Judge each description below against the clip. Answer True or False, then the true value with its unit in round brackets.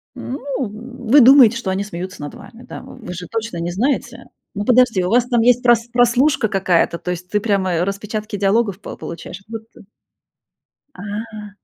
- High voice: True (215 Hz)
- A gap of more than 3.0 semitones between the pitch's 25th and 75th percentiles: True (4.0 semitones)